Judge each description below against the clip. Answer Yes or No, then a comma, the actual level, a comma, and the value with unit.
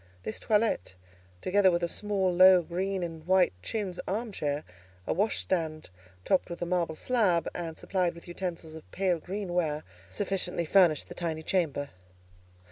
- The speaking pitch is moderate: Yes, medium, 180 Hz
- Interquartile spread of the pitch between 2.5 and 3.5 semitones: Yes, average, 2.8 semitones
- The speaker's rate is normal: Yes, average, 150 wpm